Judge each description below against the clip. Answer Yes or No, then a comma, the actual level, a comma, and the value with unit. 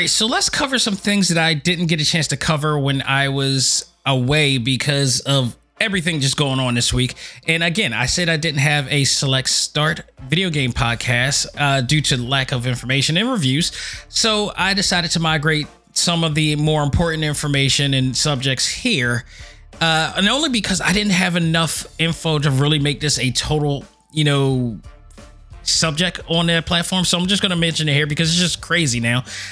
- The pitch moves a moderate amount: Yes, average, 4.0 semitones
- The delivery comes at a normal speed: Yes, average, 190 wpm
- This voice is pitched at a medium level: Yes, medium, 150 Hz